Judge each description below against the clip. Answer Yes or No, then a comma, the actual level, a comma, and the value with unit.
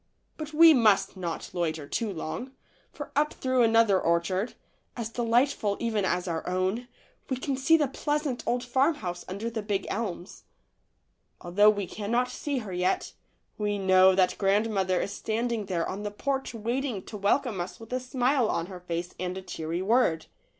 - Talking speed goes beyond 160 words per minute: Yes, average, 170 wpm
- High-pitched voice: Yes, high, 210 Hz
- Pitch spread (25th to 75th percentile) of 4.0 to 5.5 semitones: Yes, average, 5.1 semitones